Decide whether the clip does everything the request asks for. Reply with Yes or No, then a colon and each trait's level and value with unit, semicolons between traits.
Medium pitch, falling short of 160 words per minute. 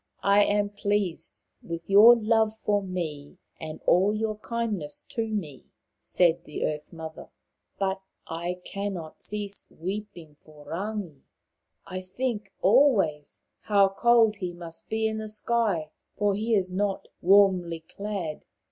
No: high, 195 Hz; average, 140 wpm